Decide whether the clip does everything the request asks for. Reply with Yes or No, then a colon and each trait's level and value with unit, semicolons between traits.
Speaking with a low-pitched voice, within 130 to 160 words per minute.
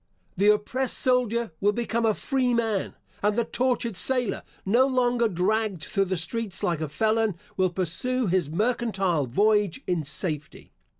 No: high, 210 Hz; average, 145 wpm